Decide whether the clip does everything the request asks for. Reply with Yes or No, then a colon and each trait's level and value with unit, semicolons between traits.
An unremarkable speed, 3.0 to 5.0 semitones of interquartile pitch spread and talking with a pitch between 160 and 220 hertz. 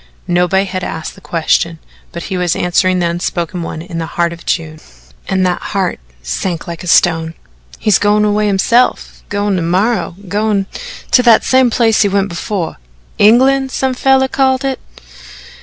Yes: average, 170 wpm; average, 4.2 semitones; high, 190 Hz